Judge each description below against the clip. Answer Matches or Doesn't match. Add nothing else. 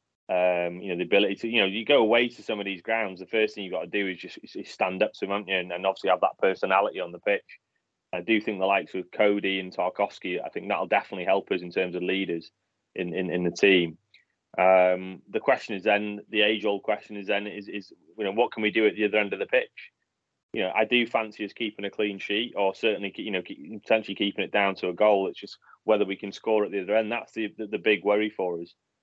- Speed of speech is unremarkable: Doesn't match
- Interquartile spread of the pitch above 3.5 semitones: Doesn't match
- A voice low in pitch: Matches